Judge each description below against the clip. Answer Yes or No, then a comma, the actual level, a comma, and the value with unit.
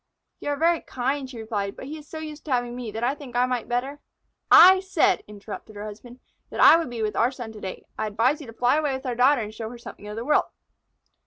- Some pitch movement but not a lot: Yes, average, 4.5 semitones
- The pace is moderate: No, fast, 270 wpm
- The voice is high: Yes, high, 245 Hz